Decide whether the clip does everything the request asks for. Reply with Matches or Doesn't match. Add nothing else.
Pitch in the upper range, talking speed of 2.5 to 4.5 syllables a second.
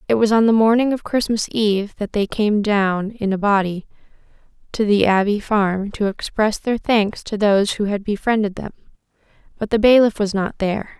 Doesn't match